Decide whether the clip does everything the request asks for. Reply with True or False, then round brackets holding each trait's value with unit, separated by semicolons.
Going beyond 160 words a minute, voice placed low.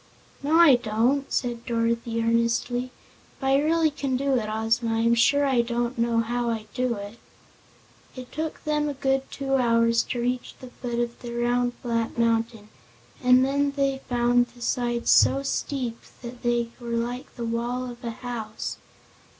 False (175 wpm; 240 Hz)